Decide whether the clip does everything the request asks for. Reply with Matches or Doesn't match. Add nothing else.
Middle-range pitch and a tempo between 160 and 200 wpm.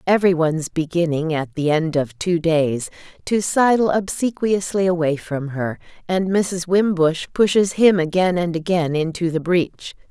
Doesn't match